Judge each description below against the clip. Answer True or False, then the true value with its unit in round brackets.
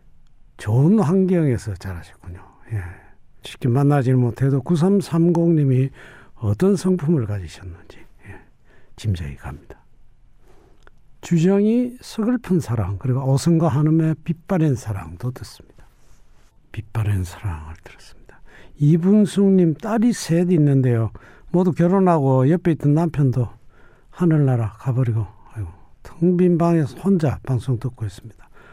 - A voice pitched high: False (135 Hz)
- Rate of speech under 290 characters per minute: True (260 characters per minute)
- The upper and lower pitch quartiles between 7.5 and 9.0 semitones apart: True (8.3 semitones)